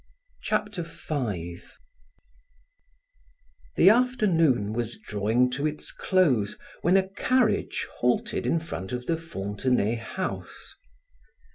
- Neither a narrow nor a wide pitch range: No, wide, 8.7 semitones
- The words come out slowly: Yes, slow, 100 wpm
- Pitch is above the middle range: No, medium, 140 Hz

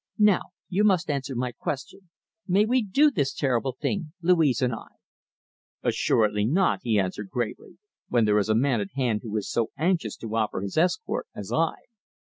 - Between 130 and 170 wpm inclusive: No, average, 180 wpm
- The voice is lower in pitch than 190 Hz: Yes, low, 135 Hz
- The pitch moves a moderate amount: No, wide, 8.4 semitones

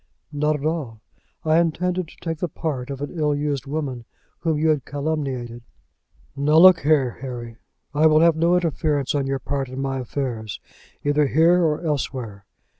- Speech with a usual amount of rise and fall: Yes, average, 3.1 semitones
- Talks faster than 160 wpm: Yes, average, 175 wpm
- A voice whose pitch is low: No, medium, 145 Hz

